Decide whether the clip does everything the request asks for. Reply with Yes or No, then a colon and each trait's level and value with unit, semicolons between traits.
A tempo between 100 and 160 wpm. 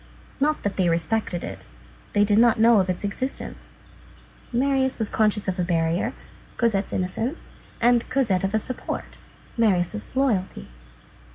Yes: average, 145 wpm